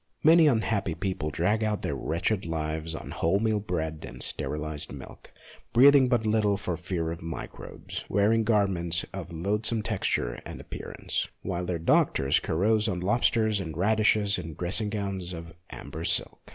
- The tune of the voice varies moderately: Yes, average, 4.7 semitones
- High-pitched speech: No, very low, 95 Hz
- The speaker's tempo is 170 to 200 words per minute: No, average, 155 wpm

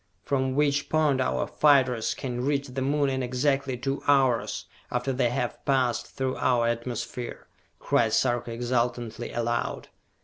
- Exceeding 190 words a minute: No, average, 140 wpm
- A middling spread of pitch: No, narrow, 2.2 semitones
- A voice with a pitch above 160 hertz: No, low, 130 Hz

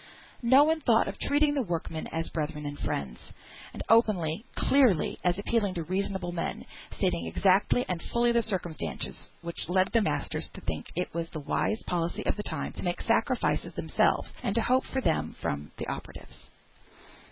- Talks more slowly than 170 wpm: No, average, 175 wpm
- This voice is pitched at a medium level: Yes, medium, 180 Hz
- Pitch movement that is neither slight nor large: No, wide, 6.0 semitones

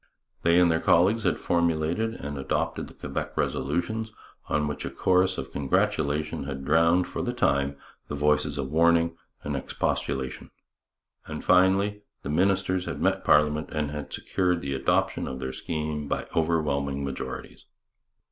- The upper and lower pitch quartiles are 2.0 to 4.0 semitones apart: Yes, average, 3.6 semitones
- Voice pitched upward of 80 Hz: No, very low, 75 Hz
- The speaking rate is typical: Yes, average, 155 wpm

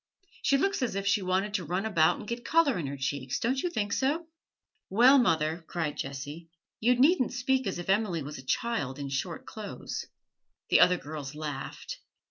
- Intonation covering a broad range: Yes, wide, 8.5 semitones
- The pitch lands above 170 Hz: Yes, high, 190 Hz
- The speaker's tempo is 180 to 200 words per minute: Yes, average, 190 wpm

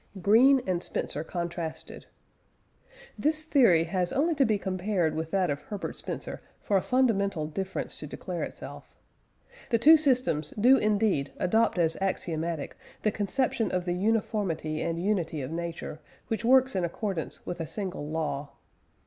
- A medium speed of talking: Yes, average, 150 wpm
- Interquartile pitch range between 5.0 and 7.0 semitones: Yes, average, 5.3 semitones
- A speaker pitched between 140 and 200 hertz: Yes, high, 190 Hz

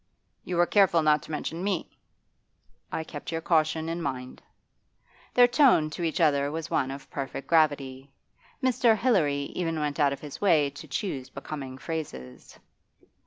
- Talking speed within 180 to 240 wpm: No, average, 160 wpm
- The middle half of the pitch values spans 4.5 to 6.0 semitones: No, average, 3.3 semitones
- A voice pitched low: No, medium, 155 Hz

